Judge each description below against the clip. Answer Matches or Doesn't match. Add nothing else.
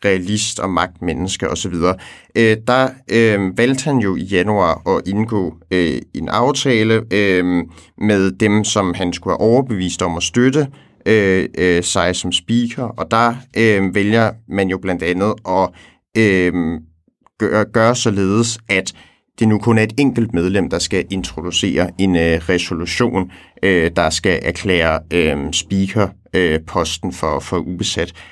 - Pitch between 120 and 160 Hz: Doesn't match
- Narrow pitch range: Doesn't match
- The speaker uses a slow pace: Doesn't match